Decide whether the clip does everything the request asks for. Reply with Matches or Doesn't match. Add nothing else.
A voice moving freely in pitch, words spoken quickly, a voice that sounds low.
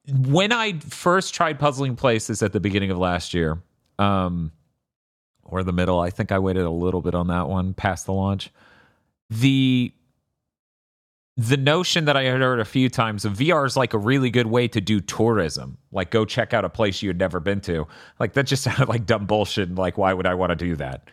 Matches